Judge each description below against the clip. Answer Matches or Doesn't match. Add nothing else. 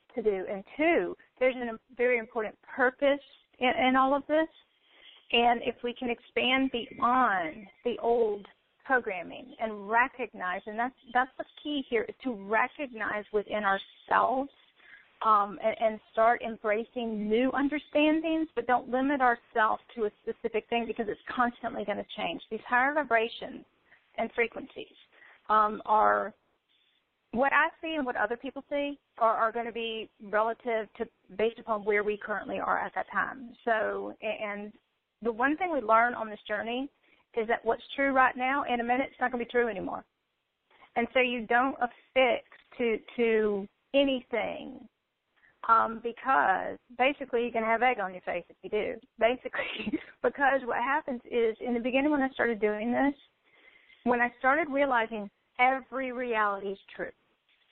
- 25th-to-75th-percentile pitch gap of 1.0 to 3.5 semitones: Matches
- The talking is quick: Doesn't match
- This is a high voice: Matches